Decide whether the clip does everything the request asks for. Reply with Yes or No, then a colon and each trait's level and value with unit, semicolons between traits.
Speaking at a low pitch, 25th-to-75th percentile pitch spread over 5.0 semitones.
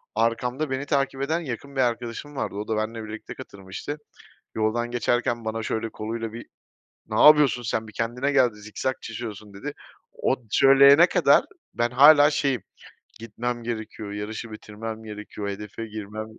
No: low, 115 Hz; average, 3.6 semitones